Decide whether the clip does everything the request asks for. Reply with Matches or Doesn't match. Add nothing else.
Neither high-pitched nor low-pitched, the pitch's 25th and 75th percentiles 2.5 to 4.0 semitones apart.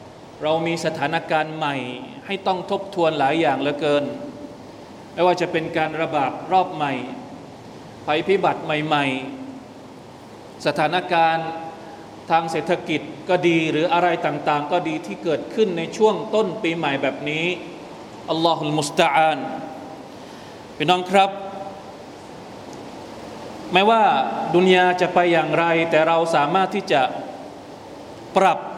Matches